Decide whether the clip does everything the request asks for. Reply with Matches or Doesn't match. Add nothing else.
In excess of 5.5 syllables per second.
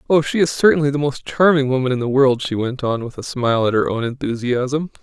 Matches